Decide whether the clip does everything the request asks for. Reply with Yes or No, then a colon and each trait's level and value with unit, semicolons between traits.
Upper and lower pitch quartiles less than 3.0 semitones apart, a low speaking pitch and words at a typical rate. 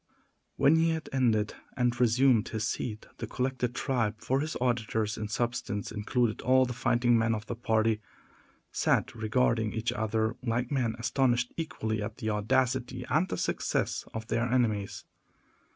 Yes: narrow, 2.6 semitones; low, 120 Hz; average, 150 wpm